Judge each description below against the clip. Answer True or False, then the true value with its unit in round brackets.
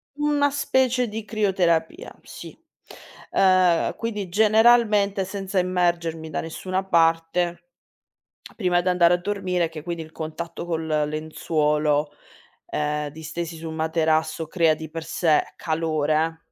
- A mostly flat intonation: False (3.2 semitones)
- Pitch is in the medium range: True (170 Hz)